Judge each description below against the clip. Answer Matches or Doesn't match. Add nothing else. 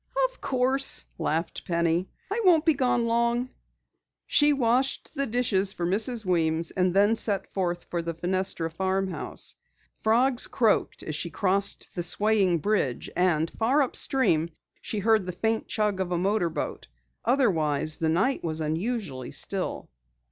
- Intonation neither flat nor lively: Doesn't match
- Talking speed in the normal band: Matches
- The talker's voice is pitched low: Doesn't match